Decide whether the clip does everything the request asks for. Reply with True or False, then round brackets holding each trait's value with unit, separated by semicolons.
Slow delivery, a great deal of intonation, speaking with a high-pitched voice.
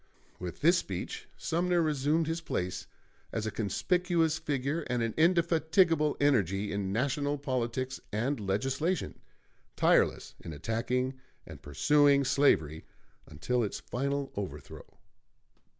False (115 wpm; 6.2 semitones; 135 Hz)